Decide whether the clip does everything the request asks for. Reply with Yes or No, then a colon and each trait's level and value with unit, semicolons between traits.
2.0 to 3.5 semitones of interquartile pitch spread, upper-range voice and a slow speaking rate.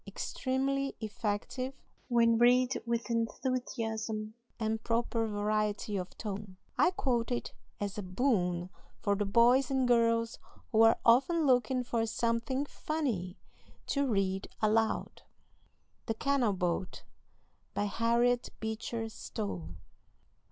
Yes: average, 3.0 semitones; high, 230 Hz; slow, 115 wpm